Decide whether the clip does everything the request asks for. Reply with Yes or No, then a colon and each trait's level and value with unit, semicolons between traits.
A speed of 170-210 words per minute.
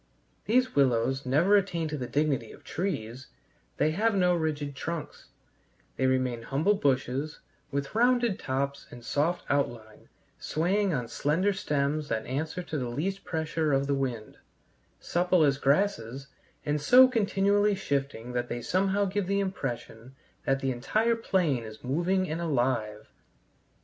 No: average, 145 wpm